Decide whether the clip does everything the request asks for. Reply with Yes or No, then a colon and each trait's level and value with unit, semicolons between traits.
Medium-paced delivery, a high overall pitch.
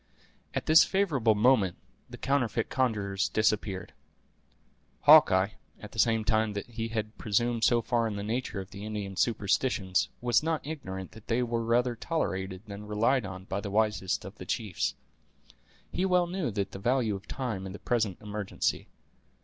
No: average, 165 wpm; low, 110 Hz